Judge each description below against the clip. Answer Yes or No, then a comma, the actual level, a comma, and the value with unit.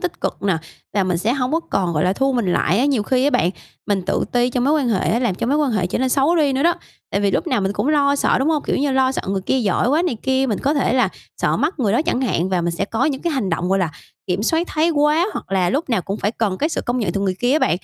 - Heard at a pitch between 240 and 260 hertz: Yes, very high, 250 Hz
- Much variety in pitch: Yes, wide, 6.6 semitones